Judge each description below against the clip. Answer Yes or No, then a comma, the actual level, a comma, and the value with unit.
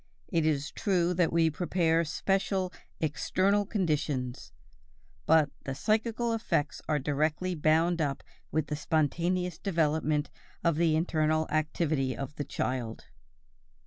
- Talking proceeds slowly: Yes, slow, 120 wpm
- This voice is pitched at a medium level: Yes, medium, 160 Hz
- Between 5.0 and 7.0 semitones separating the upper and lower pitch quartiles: No, average, 3.2 semitones